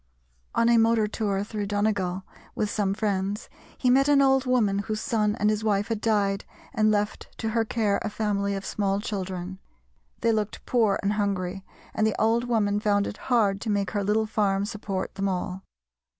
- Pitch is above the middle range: Yes, high, 210 Hz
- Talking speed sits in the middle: Yes, average, 190 wpm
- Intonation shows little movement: Yes, narrow, 1.9 semitones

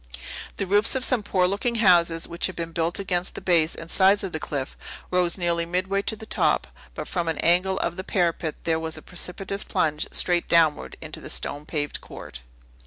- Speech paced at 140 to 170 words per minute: No, average, 200 wpm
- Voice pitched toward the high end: No, medium, 175 Hz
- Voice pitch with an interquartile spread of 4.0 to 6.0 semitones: No, average, 2.7 semitones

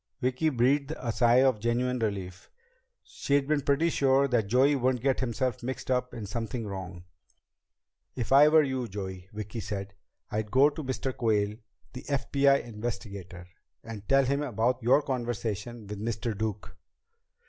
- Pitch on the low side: Yes, low, 120 Hz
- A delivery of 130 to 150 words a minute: No, average, 160 wpm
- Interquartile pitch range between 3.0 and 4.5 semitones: Yes, average, 4.1 semitones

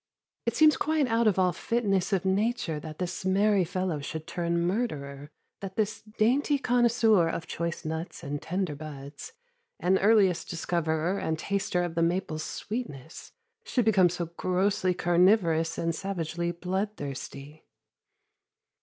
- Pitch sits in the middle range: Yes, medium, 180 Hz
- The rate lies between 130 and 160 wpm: Yes, slow, 135 wpm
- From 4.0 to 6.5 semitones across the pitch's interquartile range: Yes, average, 4.3 semitones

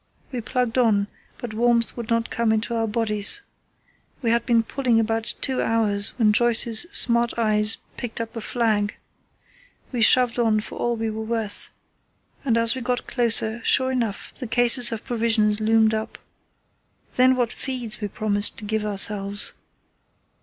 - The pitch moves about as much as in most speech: No, narrow, 1.7 semitones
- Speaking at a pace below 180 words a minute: Yes, average, 160 wpm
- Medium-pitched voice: No, high, 230 Hz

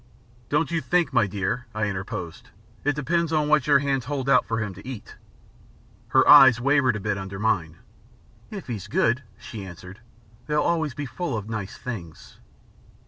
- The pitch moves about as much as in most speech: No, wide, 6.2 semitones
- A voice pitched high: No, low, 125 Hz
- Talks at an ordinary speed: Yes, average, 175 wpm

